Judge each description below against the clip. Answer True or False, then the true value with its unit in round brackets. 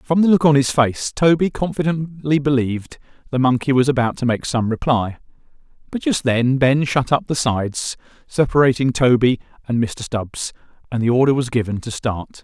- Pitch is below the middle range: True (130 Hz)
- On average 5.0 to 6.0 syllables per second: True (5.1 syllables/s)